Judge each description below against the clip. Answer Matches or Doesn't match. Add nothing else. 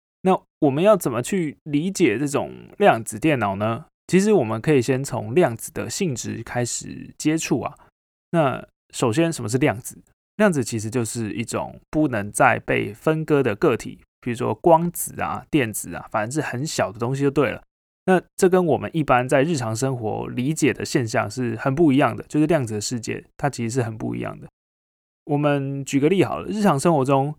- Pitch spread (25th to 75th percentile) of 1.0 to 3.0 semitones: Doesn't match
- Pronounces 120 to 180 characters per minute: Doesn't match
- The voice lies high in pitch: Doesn't match